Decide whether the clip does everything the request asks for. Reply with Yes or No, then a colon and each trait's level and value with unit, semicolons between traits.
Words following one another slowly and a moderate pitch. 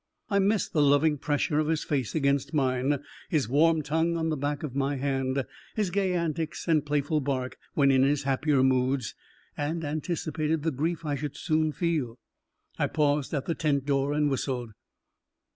No: average, 175 wpm; medium, 145 Hz